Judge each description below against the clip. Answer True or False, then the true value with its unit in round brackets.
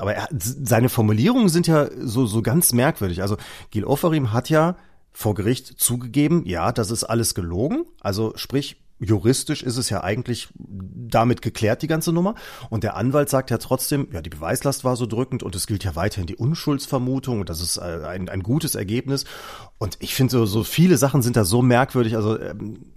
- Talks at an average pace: False (195 wpm)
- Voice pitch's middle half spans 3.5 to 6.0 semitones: True (4.4 semitones)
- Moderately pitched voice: False (120 Hz)